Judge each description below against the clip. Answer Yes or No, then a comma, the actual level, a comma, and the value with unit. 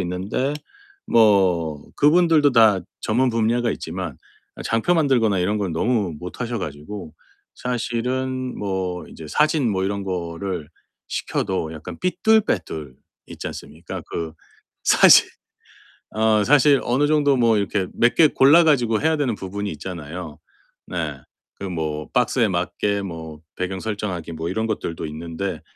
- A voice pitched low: Yes, low, 100 Hz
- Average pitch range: No, wide, 6.1 semitones